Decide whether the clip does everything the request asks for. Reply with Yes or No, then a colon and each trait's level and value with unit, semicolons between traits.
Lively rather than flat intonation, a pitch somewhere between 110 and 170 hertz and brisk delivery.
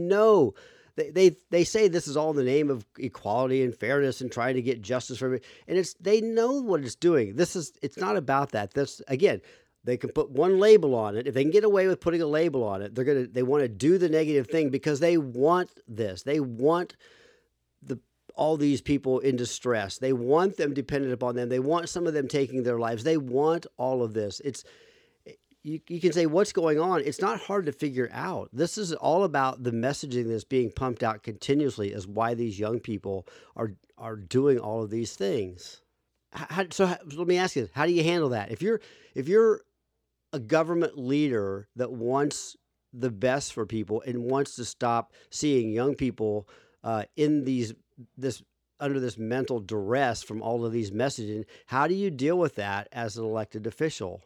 Yes: wide, 6.3 semitones; low, 135 Hz; fast, 210 wpm